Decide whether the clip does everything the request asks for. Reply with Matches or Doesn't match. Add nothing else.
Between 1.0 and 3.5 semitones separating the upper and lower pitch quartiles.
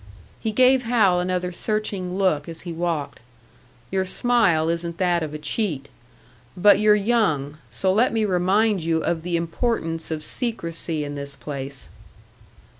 Doesn't match